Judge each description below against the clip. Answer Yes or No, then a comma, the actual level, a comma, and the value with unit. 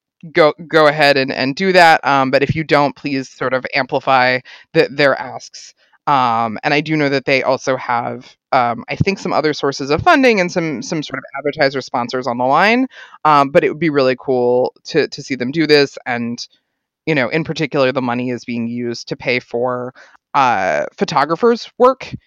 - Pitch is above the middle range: No, medium, 140 Hz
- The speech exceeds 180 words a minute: Yes, average, 200 wpm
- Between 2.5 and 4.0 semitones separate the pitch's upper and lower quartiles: Yes, average, 3.7 semitones